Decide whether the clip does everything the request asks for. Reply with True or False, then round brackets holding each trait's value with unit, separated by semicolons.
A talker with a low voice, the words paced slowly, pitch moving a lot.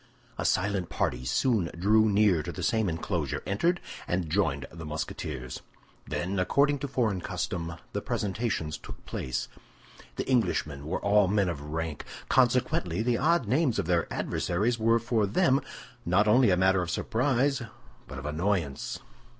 False (100 Hz; 155 wpm; 6.0 semitones)